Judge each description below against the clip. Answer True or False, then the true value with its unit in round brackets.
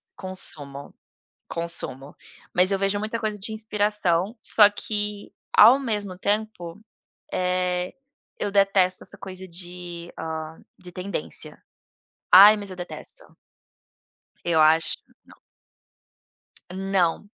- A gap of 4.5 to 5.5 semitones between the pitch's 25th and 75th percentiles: False (3.0 semitones)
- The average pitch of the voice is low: False (185 Hz)